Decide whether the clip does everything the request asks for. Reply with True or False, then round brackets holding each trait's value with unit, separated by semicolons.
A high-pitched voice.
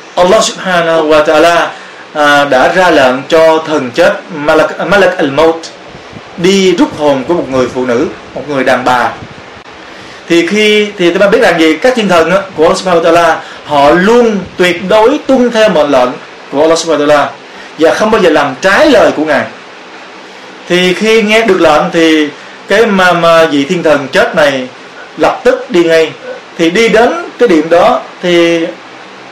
False (170 Hz)